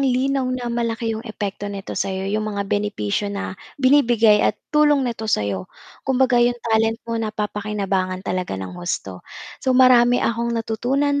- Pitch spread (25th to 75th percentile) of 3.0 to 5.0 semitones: Yes, average, 3.6 semitones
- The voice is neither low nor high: No, high, 225 Hz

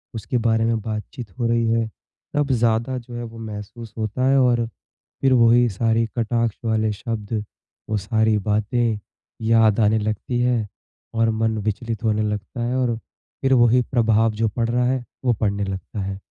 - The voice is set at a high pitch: No, low, 115 Hz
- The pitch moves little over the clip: Yes, narrow, 1.8 semitones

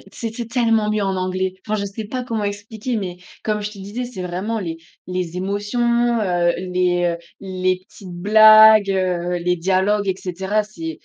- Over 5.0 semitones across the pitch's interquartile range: No, average, 2.9 semitones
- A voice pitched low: No, high, 200 Hz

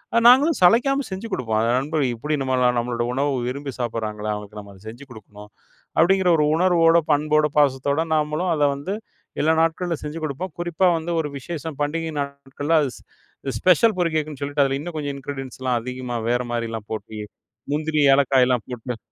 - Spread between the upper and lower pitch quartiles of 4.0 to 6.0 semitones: Yes, average, 4.7 semitones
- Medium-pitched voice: Yes, medium, 145 Hz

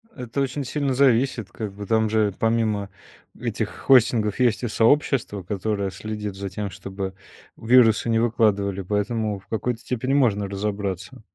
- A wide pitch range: No, average, 3.1 semitones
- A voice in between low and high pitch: No, low, 110 Hz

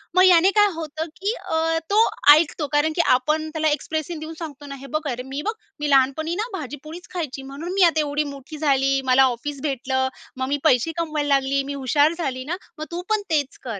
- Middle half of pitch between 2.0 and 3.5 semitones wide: Yes, average, 3.1 semitones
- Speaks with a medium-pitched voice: No, very high, 300 Hz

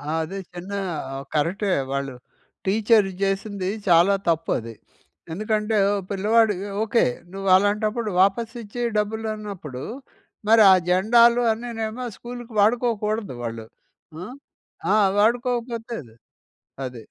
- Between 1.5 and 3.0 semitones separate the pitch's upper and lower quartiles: No, average, 3.5 semitones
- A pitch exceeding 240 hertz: No, high, 210 Hz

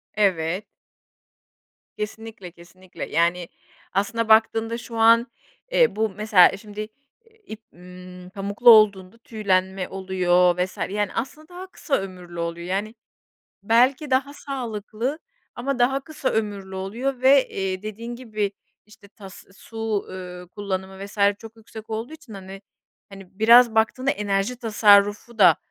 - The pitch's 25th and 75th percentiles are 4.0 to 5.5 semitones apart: No, average, 3.6 semitones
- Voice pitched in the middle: No, high, 210 Hz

